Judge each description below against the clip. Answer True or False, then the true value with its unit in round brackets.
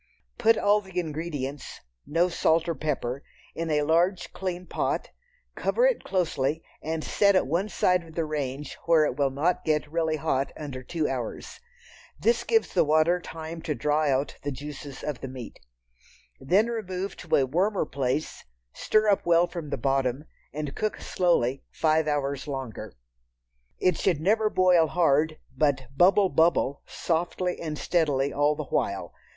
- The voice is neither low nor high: True (155 Hz)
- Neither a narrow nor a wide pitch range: True (4.0 semitones)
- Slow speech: False (160 wpm)